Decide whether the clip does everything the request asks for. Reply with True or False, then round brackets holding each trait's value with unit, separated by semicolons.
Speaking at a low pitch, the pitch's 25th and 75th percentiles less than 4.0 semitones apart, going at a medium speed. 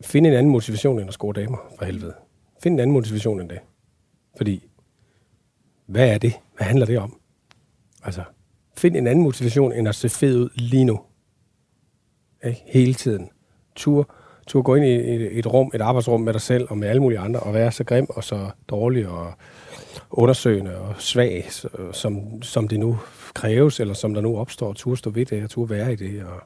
True (120 Hz; 3.1 semitones; 200 wpm)